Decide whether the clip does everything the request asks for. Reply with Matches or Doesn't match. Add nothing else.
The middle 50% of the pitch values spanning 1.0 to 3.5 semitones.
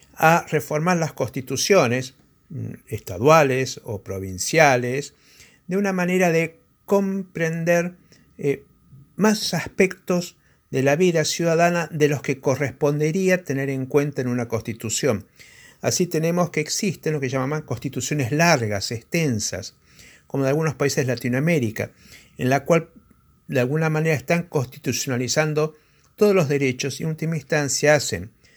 Doesn't match